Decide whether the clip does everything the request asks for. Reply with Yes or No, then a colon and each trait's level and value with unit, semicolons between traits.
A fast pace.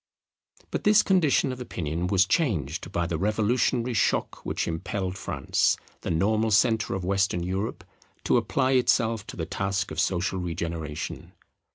No: average, 150 wpm